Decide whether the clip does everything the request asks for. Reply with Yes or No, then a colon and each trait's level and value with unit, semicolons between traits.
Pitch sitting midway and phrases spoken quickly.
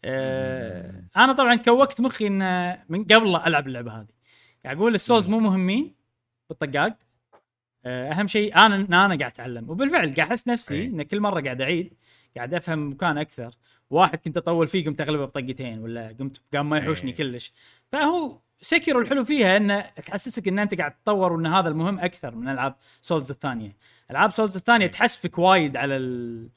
Yes: medium, 165 Hz; fast, 165 wpm